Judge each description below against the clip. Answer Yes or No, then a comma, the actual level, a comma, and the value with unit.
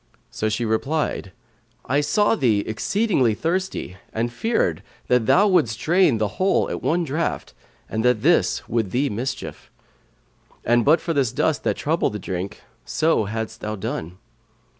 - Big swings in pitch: Yes, wide, 7.0 semitones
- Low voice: Yes, low, 120 Hz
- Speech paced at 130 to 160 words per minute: Yes, average, 155 wpm